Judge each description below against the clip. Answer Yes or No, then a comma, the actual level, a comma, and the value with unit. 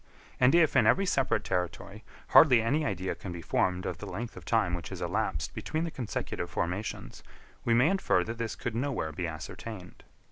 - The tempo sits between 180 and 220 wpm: Yes, average, 190 wpm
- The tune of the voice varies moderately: No, wide, 6.6 semitones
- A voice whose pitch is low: Yes, low, 115 Hz